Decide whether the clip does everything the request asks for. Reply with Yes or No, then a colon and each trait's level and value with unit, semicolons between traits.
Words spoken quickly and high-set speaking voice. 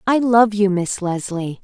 No: average, 185 wpm; high, 200 Hz